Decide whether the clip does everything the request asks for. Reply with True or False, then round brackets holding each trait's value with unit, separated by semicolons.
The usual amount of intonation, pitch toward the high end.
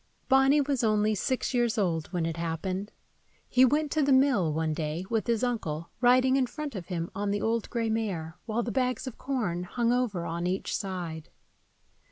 False (6.6 semitones; 215 Hz)